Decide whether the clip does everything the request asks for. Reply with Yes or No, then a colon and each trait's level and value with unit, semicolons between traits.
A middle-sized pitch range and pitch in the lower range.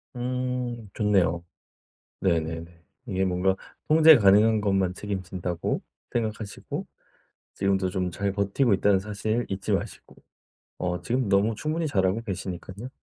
Yes: average, 3.5 semitones; low, 100 Hz